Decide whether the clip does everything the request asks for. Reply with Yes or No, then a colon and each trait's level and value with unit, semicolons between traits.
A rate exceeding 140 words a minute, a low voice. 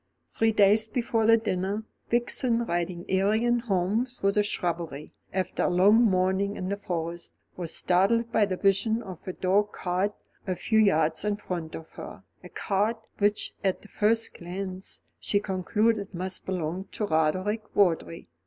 No: average, 160 wpm; high, 195 Hz